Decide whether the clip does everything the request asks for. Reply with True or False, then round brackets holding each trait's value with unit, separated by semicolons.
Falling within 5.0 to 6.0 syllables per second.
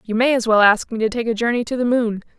False (6.6 syllables/s)